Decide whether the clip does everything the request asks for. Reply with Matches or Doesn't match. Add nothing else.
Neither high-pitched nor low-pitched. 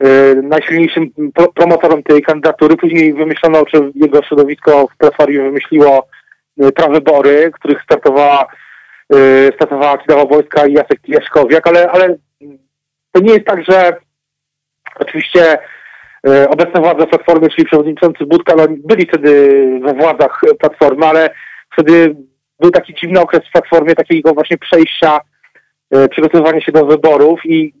Matches